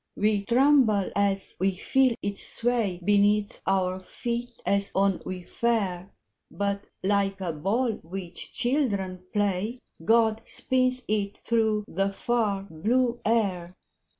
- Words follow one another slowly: Yes, slow, 125 wpm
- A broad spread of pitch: No, average, 3.3 semitones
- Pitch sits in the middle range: No, high, 205 Hz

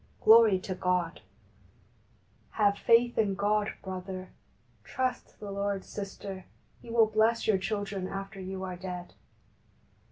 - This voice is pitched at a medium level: No, high, 200 Hz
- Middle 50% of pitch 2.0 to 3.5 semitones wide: Yes, narrow, 2.6 semitones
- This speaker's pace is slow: Yes, slow, 125 wpm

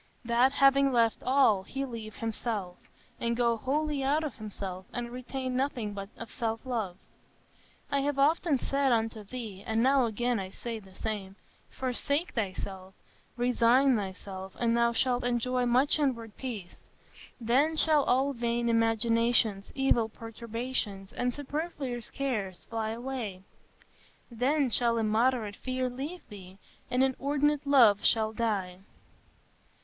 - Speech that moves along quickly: No, slow, 135 wpm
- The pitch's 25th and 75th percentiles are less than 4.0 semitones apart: Yes, average, 3.5 semitones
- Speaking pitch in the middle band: No, high, 235 Hz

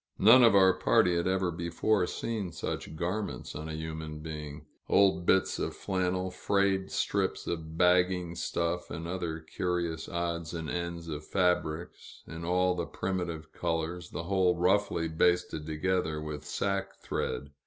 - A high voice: No, very low, 85 Hz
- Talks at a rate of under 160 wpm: Yes, average, 150 wpm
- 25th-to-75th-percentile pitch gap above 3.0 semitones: No, narrow, 2.5 semitones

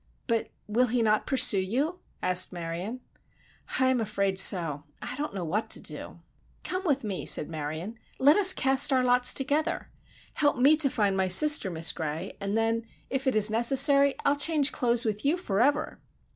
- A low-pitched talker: No, high, 235 Hz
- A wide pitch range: Yes, wide, 6.2 semitones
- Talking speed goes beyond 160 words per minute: Yes, average, 180 wpm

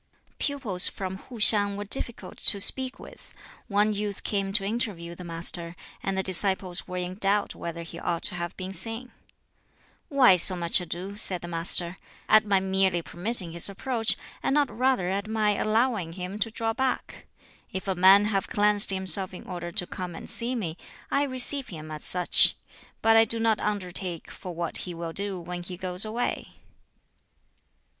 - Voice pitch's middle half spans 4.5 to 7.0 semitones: No, average, 3.4 semitones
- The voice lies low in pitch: No, high, 195 Hz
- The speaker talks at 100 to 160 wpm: No, average, 180 wpm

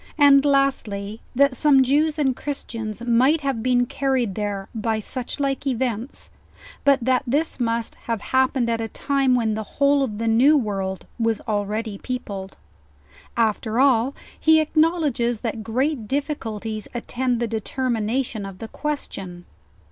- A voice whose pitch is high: Yes, high, 240 Hz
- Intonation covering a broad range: No, average, 4.0 semitones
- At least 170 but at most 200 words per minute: No, average, 145 wpm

